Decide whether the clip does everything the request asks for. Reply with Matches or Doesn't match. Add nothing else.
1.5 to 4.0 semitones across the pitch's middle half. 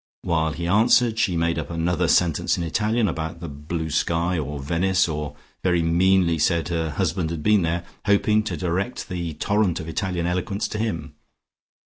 Matches